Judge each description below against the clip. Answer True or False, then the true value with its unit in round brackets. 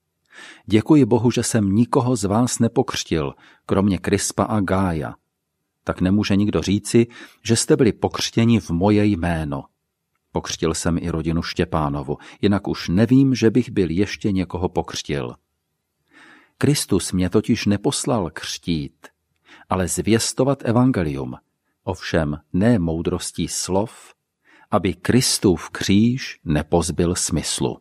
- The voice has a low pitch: True (100 Hz)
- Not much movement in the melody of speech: False (5.5 semitones)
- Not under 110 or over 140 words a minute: True (115 wpm)